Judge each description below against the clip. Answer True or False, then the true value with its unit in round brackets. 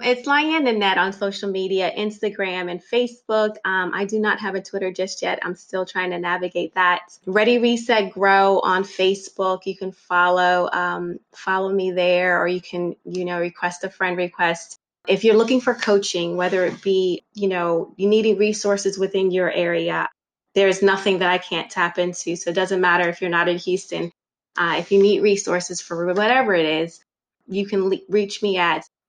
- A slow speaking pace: False (190 wpm)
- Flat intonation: True (2.1 semitones)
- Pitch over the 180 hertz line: True (190 Hz)